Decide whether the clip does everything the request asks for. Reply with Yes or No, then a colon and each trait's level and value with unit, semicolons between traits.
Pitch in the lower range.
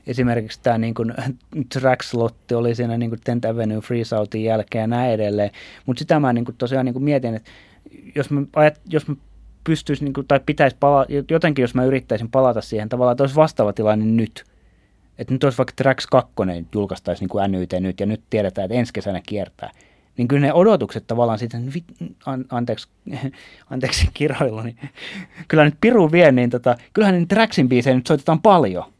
Yes: low, 125 Hz